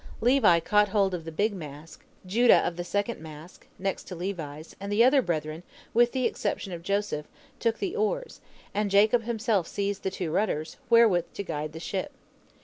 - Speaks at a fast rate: No, average, 185 wpm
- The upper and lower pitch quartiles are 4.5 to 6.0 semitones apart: Yes, average, 5.1 semitones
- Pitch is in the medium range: No, high, 200 Hz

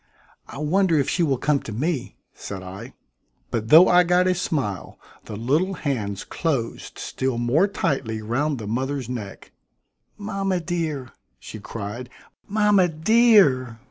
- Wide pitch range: Yes, wide, 7.2 semitones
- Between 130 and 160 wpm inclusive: Yes, average, 140 wpm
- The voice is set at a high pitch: No, medium, 140 Hz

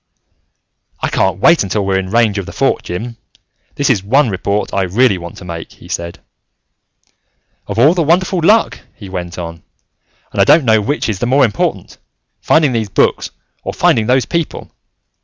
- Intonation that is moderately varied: No, wide, 6.5 semitones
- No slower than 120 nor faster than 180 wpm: No, average, 190 wpm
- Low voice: Yes, low, 110 Hz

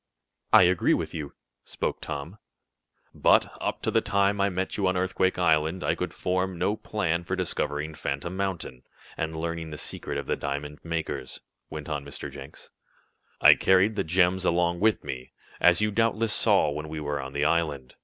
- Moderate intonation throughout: Yes, average, 3.9 semitones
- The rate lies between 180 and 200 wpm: Yes, average, 185 wpm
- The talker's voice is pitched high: No, very low, 85 Hz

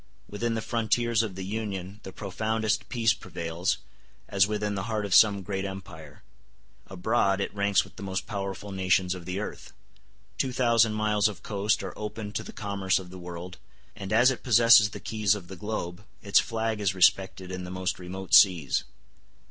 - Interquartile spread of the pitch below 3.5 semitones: Yes, narrow, 2.6 semitones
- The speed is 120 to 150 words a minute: No, average, 185 wpm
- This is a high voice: No, low, 100 Hz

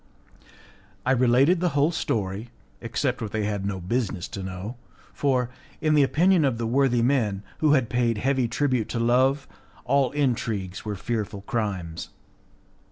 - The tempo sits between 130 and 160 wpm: Yes, average, 155 wpm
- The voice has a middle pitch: No, low, 120 Hz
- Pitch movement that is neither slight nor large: Yes, average, 4.6 semitones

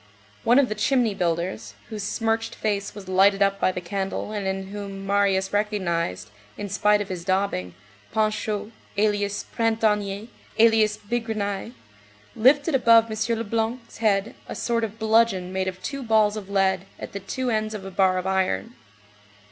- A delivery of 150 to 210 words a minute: Yes, average, 165 wpm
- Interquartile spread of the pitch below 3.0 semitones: Yes, narrow, 2.6 semitones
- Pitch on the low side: No, high, 205 Hz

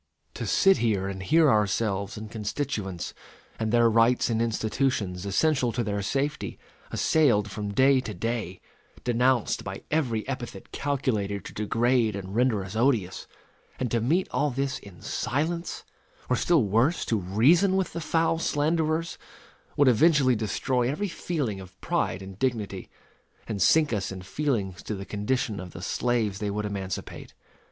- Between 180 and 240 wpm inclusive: No, average, 155 wpm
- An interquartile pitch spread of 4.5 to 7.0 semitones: Yes, wide, 5.5 semitones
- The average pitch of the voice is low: Yes, low, 115 Hz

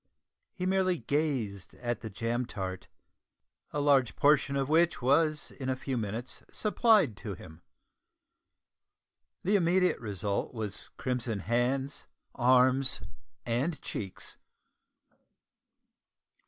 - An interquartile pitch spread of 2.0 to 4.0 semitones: No, average, 5.1 semitones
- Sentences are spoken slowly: Yes, slow, 105 wpm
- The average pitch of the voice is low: Yes, low, 130 Hz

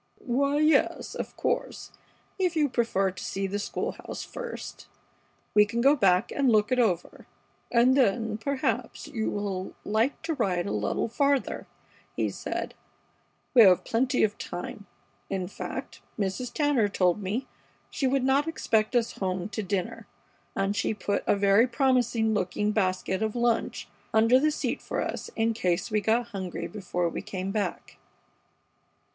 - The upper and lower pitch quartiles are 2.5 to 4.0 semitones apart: No, average, 4.4 semitones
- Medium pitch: No, high, 220 Hz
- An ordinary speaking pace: Yes, average, 160 wpm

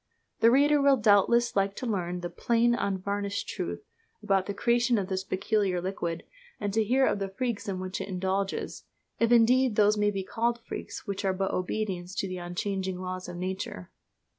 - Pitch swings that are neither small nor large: Yes, average, 3.5 semitones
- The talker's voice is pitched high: Yes, high, 200 Hz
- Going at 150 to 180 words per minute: No, average, 190 wpm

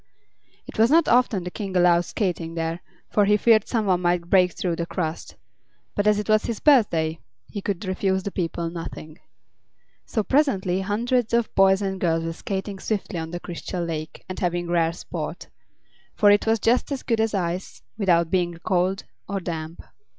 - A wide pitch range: No, average, 3.5 semitones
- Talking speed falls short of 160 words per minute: No, average, 185 wpm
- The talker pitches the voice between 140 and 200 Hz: Yes, high, 190 Hz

